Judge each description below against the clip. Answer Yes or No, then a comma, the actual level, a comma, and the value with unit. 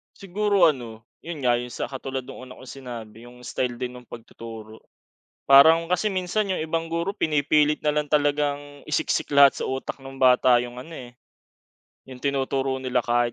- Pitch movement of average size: Yes, average, 4.0 semitones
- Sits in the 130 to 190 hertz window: Yes, low, 135 Hz